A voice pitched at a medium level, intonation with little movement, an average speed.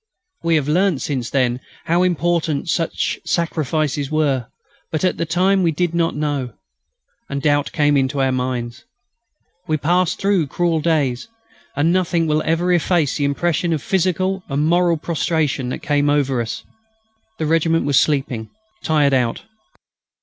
No: medium, 155 Hz; average, 3.5 semitones; average, 150 wpm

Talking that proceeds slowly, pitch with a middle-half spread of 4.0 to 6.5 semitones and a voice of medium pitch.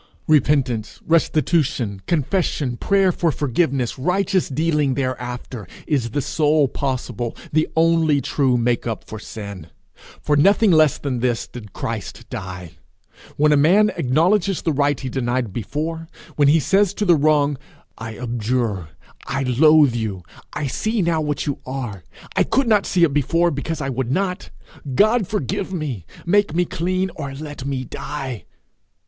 No: average, 155 wpm; average, 5.1 semitones; medium, 145 Hz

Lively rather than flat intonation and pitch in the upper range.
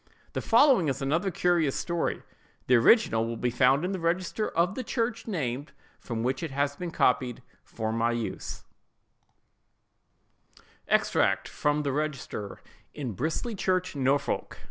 No: wide, 6.1 semitones; medium, 145 Hz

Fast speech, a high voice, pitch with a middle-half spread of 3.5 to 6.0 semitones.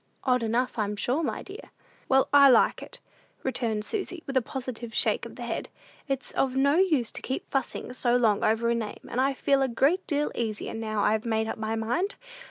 Yes: fast, 210 wpm; very high, 250 Hz; average, 3.8 semitones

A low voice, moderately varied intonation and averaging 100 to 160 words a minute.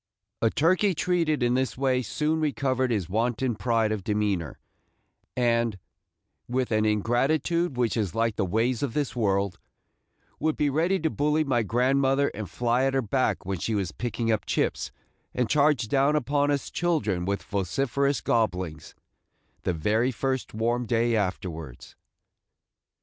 Yes: low, 120 Hz; average, 4.7 semitones; average, 150 wpm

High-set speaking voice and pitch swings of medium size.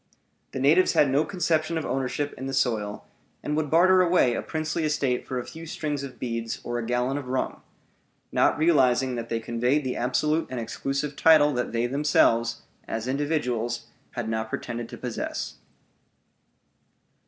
No: low, 135 Hz; average, 4.0 semitones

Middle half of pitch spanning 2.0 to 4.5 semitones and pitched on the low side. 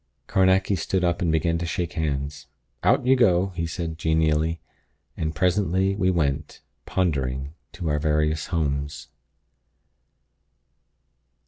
Yes: average, 3.2 semitones; very low, 80 Hz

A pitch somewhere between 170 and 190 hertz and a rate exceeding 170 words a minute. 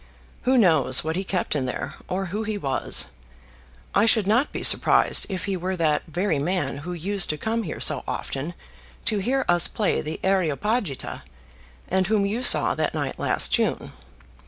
Yes: medium, 185 Hz; average, 180 wpm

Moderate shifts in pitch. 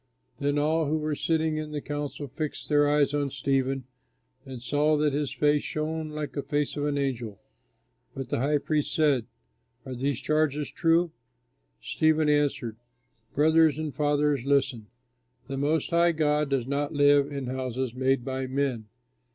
No: narrow, 2.1 semitones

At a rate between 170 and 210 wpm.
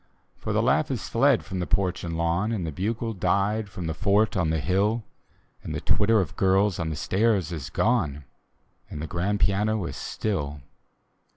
Yes: average, 190 wpm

